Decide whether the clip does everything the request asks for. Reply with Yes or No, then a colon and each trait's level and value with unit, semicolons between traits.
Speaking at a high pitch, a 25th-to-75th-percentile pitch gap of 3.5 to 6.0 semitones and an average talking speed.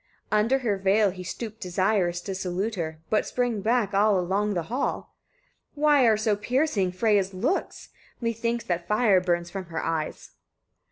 Yes: high, 200 Hz; average, 3.9 semitones; average, 160 wpm